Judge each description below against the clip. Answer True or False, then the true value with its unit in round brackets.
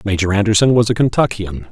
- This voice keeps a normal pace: True (175 wpm)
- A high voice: False (105 Hz)